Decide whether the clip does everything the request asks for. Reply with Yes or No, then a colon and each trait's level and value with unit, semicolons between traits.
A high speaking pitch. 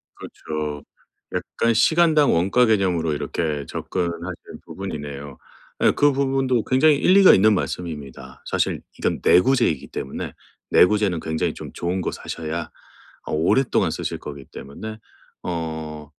No: very low, 85 Hz